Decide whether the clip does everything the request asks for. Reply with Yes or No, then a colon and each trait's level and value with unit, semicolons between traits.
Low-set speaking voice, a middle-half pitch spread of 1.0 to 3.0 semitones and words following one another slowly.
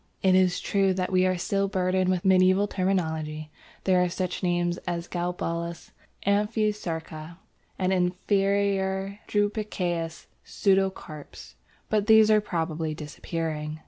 No: medium, 185 Hz; narrow, 2.6 semitones; slow, 115 wpm